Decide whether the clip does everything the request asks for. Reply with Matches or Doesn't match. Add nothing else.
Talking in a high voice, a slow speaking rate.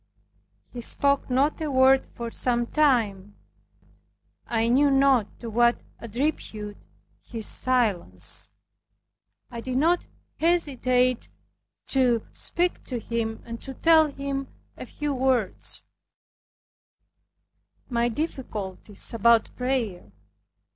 Matches